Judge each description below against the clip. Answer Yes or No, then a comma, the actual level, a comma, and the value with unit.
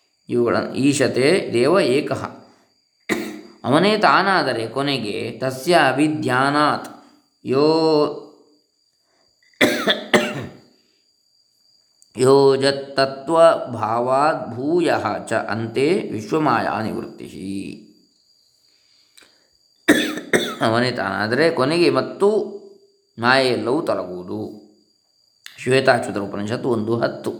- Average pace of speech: No, slow, 45 wpm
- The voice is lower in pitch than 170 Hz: Yes, low, 135 Hz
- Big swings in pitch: No, average, 4.9 semitones